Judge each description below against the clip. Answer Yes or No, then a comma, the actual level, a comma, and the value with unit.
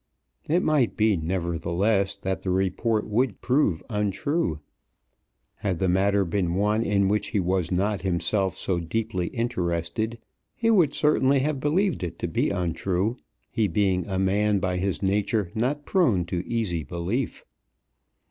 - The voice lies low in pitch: Yes, low, 100 Hz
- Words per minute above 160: No, average, 145 wpm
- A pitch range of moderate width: Yes, average, 4.2 semitones